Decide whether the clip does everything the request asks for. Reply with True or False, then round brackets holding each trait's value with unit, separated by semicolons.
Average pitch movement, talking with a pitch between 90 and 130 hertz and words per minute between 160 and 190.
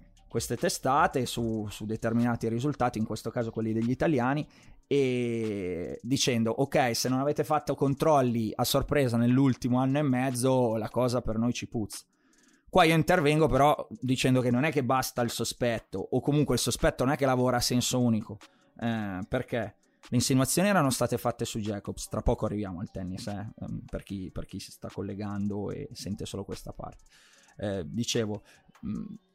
True (3.6 semitones; 120 Hz; 170 wpm)